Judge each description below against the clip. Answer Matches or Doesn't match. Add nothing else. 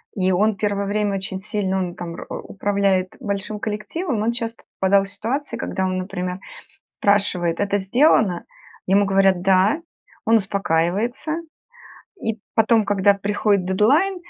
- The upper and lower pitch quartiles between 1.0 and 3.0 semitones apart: Matches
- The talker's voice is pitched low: Doesn't match